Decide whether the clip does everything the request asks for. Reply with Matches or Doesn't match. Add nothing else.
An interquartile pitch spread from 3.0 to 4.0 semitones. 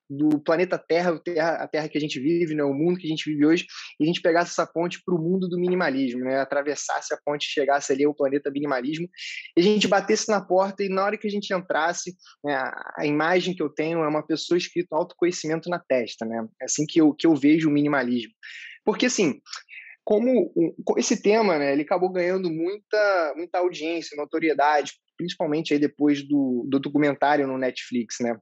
Matches